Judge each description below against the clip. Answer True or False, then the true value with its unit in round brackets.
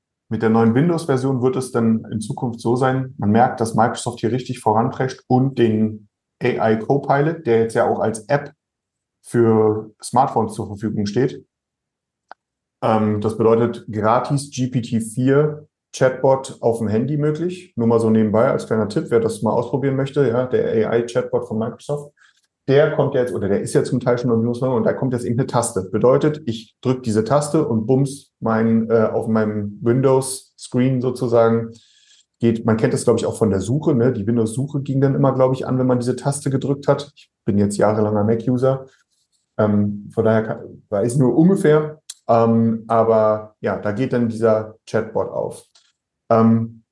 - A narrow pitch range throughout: False (3.0 semitones)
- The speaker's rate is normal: True (175 wpm)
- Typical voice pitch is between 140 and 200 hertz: False (120 Hz)